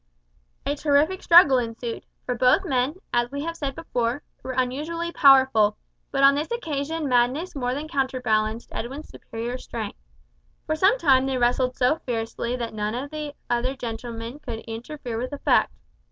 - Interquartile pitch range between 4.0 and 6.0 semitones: No, average, 3.6 semitones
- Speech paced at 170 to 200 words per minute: No, average, 160 wpm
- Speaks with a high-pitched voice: Yes, very high, 260 Hz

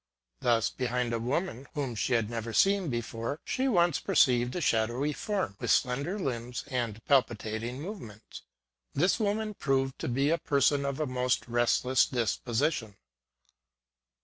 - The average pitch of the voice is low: Yes, low, 130 Hz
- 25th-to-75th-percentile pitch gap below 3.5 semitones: No, average, 4.2 semitones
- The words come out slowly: No, average, 150 wpm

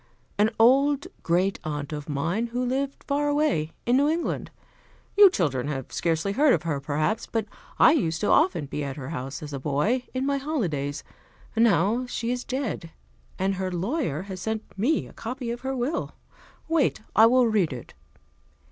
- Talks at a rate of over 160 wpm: Yes, average, 180 wpm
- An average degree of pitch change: No, wide, 8.9 semitones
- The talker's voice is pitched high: Yes, high, 215 Hz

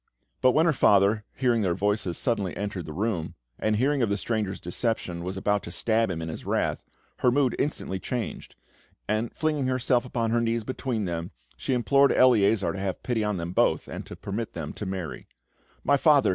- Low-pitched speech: Yes, low, 110 Hz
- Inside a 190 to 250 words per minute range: Yes, average, 200 wpm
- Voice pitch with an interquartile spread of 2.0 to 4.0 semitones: No, average, 4.6 semitones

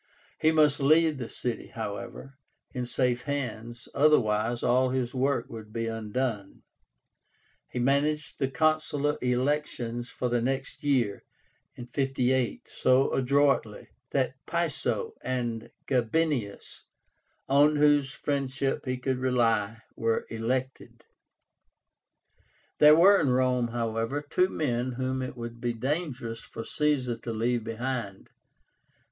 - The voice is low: Yes, low, 125 Hz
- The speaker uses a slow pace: Yes, slow, 115 wpm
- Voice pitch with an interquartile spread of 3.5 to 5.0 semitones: No, average, 3.1 semitones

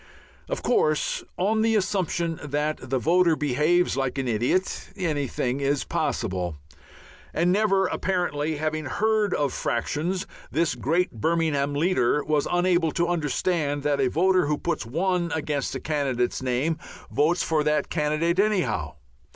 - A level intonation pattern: No, average, 4.1 semitones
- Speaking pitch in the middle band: Yes, medium, 155 Hz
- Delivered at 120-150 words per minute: Yes, average, 140 wpm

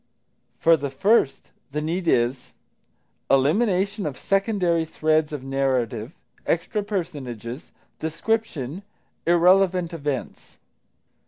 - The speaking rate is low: Yes, slow, 90 wpm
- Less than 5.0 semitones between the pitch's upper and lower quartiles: No, wide, 5.6 semitones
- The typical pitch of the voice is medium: Yes, medium, 160 Hz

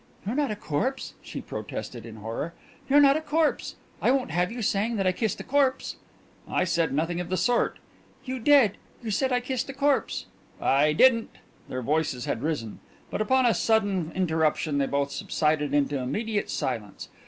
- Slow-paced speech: No, average, 185 wpm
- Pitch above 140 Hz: Yes, high, 190 Hz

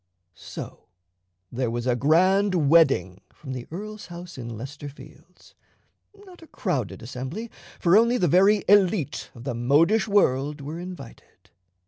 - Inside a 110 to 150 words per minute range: Yes, average, 140 wpm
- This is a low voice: No, medium, 160 Hz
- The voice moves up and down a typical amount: No, wide, 7.2 semitones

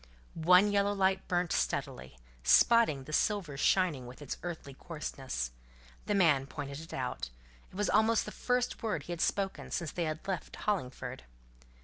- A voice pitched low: No, medium, 170 Hz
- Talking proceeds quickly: No, average, 160 wpm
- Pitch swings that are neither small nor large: No, wide, 6.3 semitones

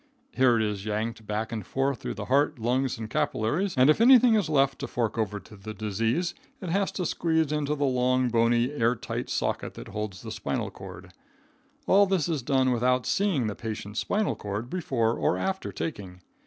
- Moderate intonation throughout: No, wide, 5.8 semitones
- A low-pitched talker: Yes, low, 125 Hz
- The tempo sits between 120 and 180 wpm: No, average, 195 wpm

